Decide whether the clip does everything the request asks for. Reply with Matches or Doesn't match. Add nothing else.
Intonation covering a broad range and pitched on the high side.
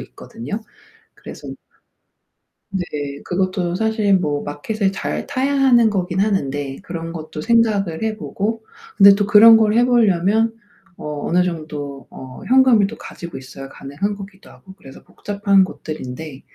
Matches